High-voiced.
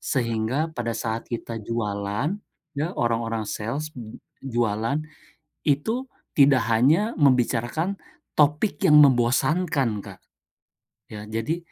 No: low, 125 Hz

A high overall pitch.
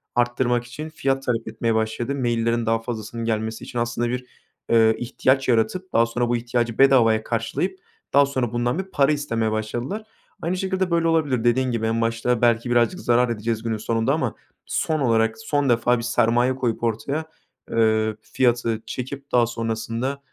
No: low, 120 Hz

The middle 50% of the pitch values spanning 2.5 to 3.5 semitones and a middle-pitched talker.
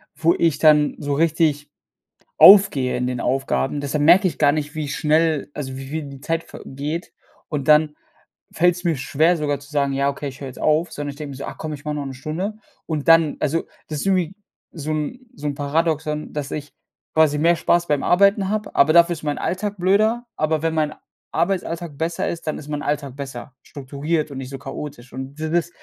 Yes: average, 2.8 semitones; medium, 150 Hz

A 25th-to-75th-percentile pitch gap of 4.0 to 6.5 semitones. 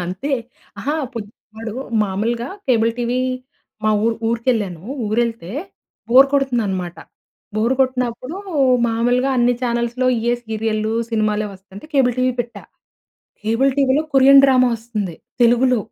No: average, 2.8 semitones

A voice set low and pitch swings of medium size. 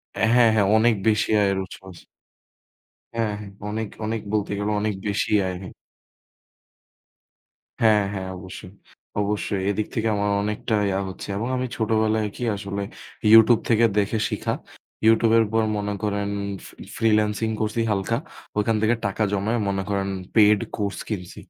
No: low, 105 Hz; narrow, 1.8 semitones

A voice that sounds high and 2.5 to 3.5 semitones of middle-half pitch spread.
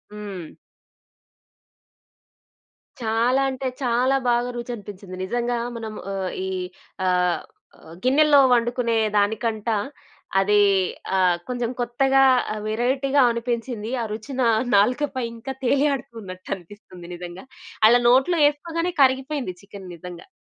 No: high, 235 Hz; average, 4.4 semitones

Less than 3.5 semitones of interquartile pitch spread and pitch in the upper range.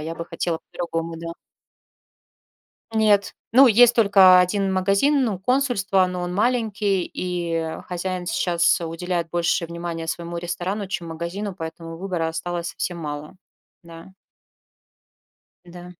No: average, 2.8 semitones; medium, 180 Hz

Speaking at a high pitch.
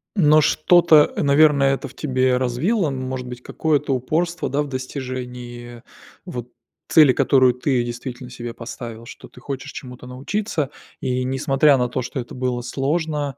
No: low, 130 Hz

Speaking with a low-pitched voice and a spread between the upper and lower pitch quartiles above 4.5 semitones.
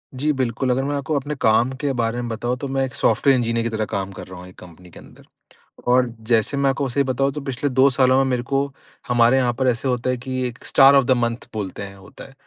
No: low, 125 Hz; narrow, 2.6 semitones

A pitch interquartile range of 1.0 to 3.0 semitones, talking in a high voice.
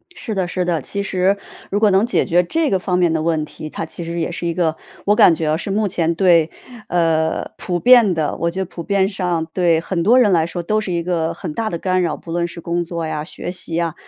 No: narrow, 2.6 semitones; medium, 175 Hz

